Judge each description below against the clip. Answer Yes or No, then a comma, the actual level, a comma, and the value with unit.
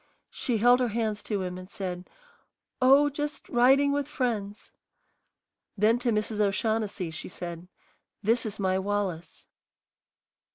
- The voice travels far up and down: No, average, 4.3 semitones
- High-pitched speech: Yes, high, 215 Hz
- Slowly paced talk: Yes, slow, 130 wpm